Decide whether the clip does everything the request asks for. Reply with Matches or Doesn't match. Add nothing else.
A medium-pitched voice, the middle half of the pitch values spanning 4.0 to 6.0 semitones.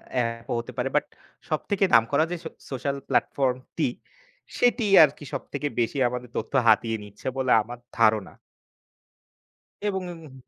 Doesn't match